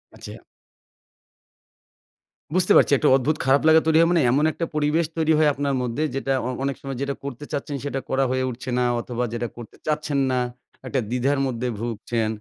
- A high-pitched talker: No, medium, 140 Hz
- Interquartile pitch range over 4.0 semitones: No, average, 3.2 semitones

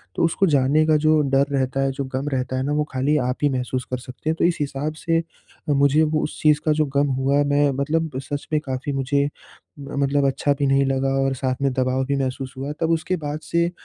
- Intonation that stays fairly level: Yes, narrow, 2.3 semitones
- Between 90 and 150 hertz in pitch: Yes, medium, 140 Hz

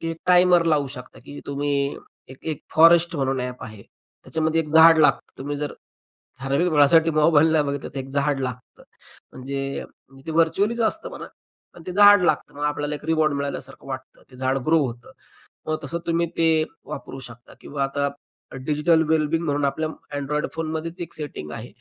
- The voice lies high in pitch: No, medium, 150 Hz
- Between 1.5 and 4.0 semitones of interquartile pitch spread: Yes, average, 3.0 semitones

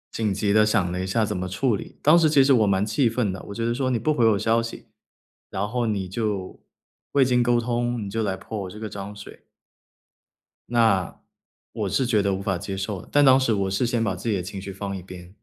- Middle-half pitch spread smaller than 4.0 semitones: Yes, average, 3.5 semitones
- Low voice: Yes, low, 105 Hz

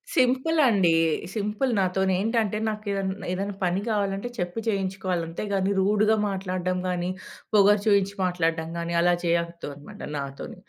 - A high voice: Yes, high, 195 Hz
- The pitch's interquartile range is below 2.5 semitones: No, average, 2.8 semitones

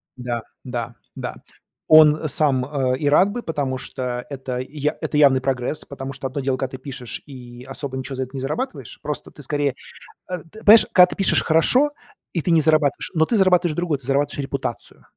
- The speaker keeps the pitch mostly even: No, average, 3.3 semitones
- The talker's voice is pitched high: No, medium, 140 Hz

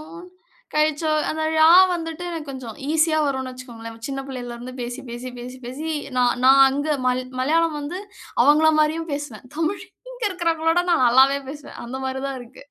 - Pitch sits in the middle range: No, very high, 280 Hz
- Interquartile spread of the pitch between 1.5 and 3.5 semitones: No, average, 3.9 semitones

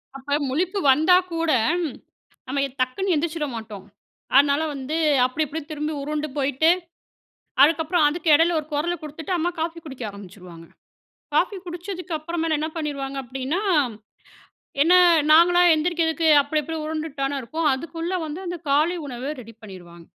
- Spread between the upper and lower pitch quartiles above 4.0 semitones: No, average, 3.5 semitones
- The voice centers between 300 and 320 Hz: Yes, very high, 305 Hz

